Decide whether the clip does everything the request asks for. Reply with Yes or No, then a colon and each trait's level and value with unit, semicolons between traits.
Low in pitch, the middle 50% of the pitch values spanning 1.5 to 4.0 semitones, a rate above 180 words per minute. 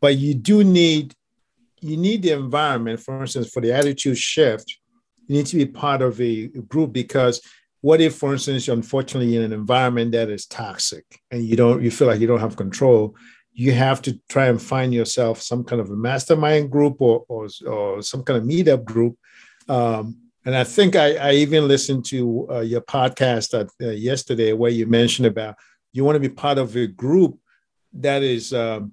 Yes: low, 130 Hz; average, 3.6 semitones; average, 195 wpm